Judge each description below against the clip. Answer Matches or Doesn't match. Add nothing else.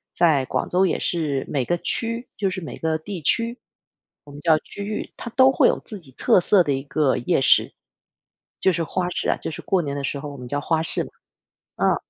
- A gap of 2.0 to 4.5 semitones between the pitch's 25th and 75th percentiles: Doesn't match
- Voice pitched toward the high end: Doesn't match